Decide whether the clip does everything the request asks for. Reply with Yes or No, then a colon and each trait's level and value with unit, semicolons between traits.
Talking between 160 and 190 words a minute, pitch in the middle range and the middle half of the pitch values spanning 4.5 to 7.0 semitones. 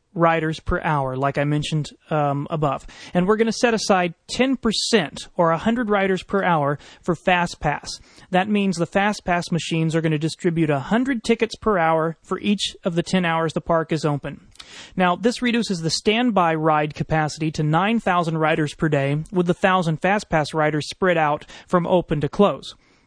No: average, 185 wpm; medium, 170 Hz; average, 4.0 semitones